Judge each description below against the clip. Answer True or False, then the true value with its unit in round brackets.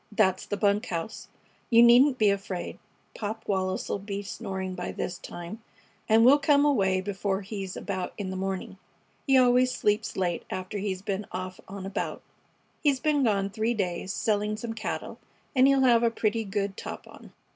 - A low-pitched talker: False (205 Hz)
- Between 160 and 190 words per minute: True (180 wpm)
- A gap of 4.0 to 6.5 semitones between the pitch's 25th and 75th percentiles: False (3.3 semitones)